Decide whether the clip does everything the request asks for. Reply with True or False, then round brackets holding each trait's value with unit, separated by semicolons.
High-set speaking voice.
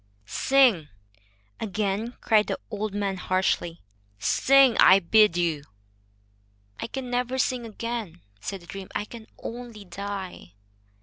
True (210 Hz)